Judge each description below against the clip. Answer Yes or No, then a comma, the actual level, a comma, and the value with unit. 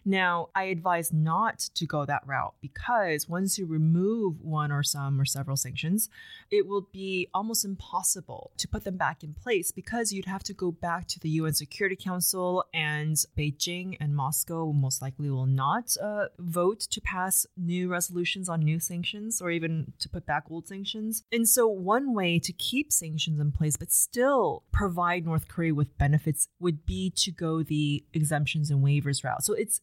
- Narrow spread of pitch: No, average, 4.2 semitones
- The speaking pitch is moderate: Yes, medium, 175 Hz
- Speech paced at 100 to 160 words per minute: No, average, 185 wpm